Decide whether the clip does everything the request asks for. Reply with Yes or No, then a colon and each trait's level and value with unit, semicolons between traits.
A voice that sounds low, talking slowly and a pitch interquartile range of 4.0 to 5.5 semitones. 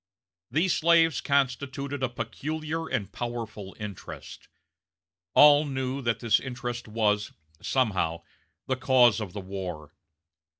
Yes: low, 125 Hz; slow, 115 wpm; average, 4.9 semitones